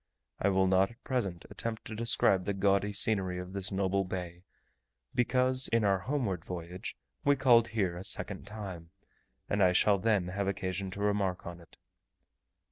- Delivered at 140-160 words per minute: No, average, 170 wpm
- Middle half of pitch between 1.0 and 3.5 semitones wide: Yes, average, 3.0 semitones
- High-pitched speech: No, low, 100 Hz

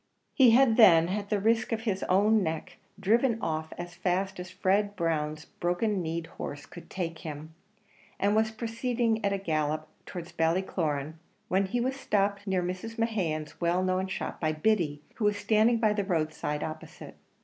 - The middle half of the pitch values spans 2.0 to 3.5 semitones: No, average, 4.9 semitones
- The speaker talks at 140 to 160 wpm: No, average, 175 wpm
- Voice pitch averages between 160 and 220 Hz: Yes, high, 190 Hz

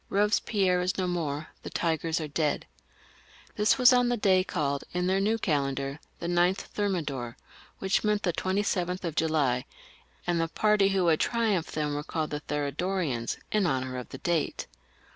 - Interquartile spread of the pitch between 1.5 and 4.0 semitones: No, average, 4.8 semitones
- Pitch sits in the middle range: Yes, medium, 175 Hz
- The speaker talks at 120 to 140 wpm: No, average, 180 wpm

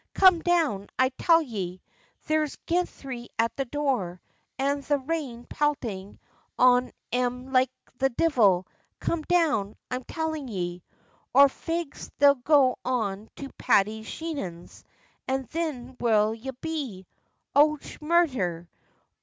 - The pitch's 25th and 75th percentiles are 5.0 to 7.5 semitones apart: Yes, wide, 5.5 semitones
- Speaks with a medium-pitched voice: No, very high, 260 Hz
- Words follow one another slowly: Yes, slow, 120 wpm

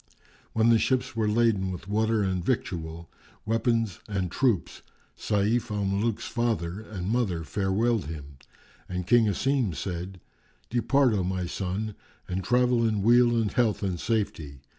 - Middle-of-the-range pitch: No, low, 105 Hz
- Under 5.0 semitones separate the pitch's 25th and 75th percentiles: Yes, average, 4.1 semitones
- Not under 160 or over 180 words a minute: No, average, 145 wpm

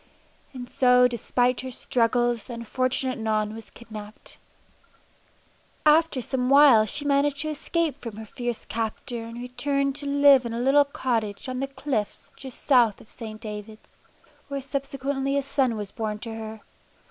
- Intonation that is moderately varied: Yes, average, 3.6 semitones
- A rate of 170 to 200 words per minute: No, average, 160 wpm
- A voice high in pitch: Yes, very high, 250 Hz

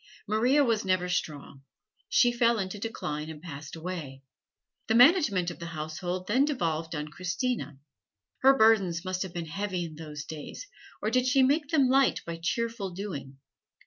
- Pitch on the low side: No, medium, 185 Hz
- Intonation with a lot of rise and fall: Yes, wide, 6.5 semitones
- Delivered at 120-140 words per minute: No, average, 170 wpm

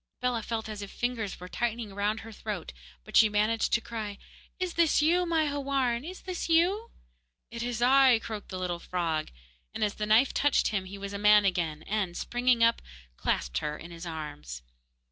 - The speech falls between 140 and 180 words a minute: No, average, 200 wpm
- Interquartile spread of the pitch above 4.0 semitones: Yes, average, 4.5 semitones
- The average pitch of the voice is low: No, high, 220 Hz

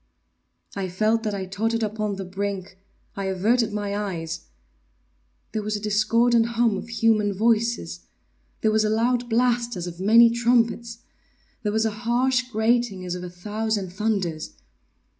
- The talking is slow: No, average, 150 wpm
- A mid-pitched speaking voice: No, high, 215 Hz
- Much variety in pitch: No, average, 3.0 semitones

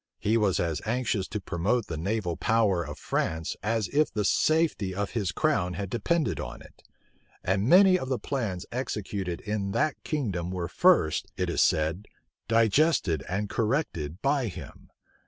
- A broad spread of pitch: Yes, wide, 6.1 semitones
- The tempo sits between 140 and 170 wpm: Yes, average, 160 wpm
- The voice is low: Yes, low, 105 Hz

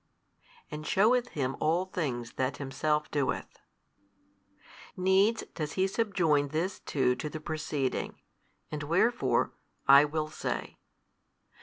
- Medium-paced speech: No, slow, 115 wpm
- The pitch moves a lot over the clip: No, average, 4.6 semitones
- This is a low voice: No, medium, 155 Hz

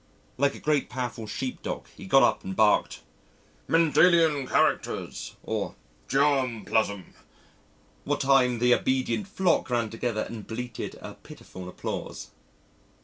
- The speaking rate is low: Yes, slow, 130 wpm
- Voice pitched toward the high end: No, low, 125 Hz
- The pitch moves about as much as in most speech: Yes, average, 4.2 semitones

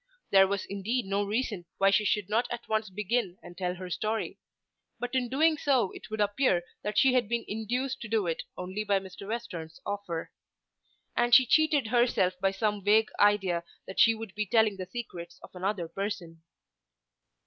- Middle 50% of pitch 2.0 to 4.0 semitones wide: Yes, average, 3.7 semitones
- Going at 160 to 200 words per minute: Yes, average, 185 wpm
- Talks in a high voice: Yes, high, 210 Hz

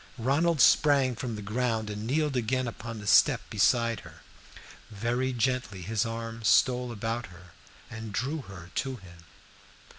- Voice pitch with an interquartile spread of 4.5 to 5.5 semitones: No, average, 3.4 semitones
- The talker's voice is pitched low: Yes, low, 115 Hz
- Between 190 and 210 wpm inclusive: No, average, 150 wpm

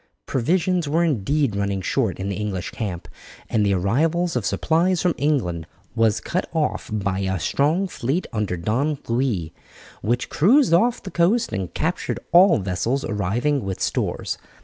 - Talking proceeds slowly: No, average, 155 wpm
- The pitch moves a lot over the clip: Yes, wide, 8.9 semitones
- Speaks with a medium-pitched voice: No, low, 125 Hz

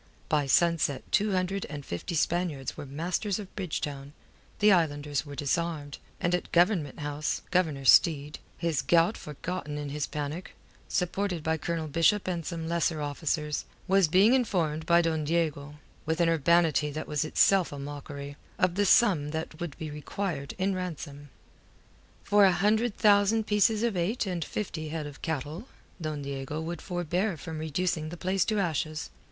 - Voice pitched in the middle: Yes, medium, 165 Hz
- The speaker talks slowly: No, average, 165 wpm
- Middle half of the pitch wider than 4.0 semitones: No, average, 3.7 semitones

